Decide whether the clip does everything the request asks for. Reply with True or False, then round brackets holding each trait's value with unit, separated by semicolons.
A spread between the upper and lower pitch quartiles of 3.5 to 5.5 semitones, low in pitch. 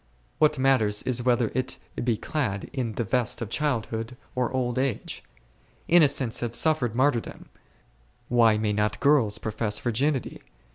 False (3.1 semitones; 120 Hz)